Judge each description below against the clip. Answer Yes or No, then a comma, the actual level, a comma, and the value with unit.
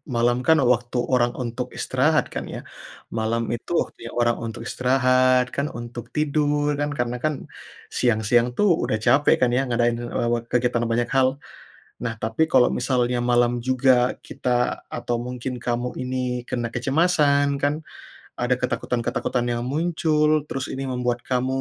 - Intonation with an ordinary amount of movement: No, narrow, 2.2 semitones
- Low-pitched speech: Yes, low, 125 Hz